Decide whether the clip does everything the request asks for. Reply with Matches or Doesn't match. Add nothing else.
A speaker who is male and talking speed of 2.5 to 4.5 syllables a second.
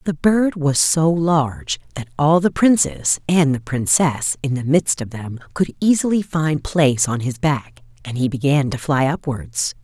Doesn't match